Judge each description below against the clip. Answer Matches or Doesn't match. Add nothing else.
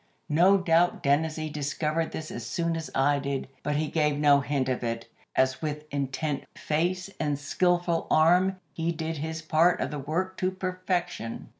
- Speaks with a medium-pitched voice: Matches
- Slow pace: Doesn't match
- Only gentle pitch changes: Doesn't match